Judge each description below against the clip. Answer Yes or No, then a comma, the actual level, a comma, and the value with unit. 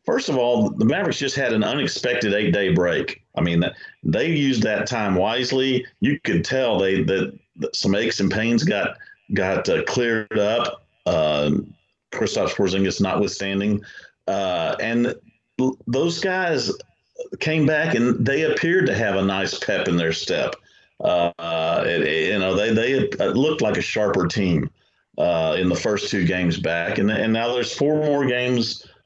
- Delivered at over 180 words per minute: No, average, 170 wpm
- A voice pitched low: Yes, low, 115 Hz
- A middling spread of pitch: No, wide, 6.1 semitones